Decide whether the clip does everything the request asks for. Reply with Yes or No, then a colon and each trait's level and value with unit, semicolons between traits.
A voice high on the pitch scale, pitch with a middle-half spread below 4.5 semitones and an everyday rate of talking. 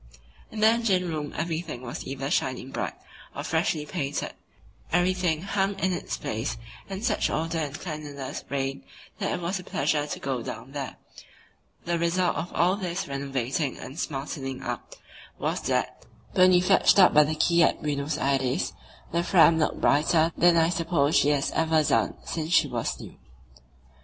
No: medium, 160 Hz; average, 4.0 semitones; average, 170 wpm